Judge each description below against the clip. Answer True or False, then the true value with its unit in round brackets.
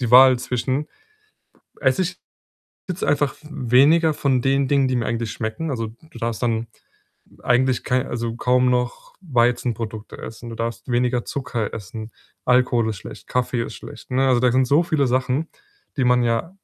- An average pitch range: False (2.3 semitones)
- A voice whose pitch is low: True (125 Hz)